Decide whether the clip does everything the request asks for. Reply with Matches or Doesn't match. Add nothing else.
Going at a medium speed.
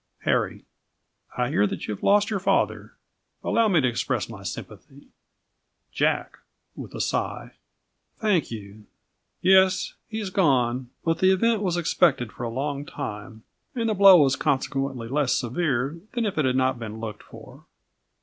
Matches